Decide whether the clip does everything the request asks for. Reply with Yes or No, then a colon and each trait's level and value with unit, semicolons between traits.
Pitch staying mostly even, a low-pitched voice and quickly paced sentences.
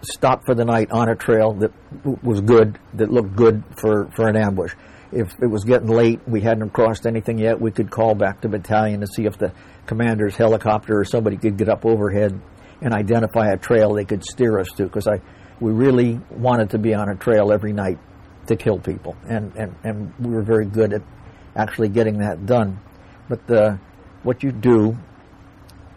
No: narrow, 1.9 semitones; low, 110 Hz; average, 195 wpm